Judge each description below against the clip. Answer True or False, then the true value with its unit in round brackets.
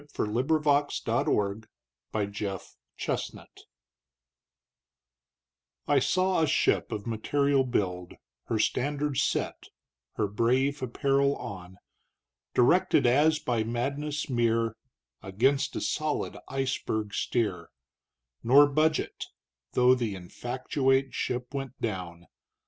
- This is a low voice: True (125 Hz)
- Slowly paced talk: True (105 wpm)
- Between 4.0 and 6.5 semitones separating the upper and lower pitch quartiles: True (4.6 semitones)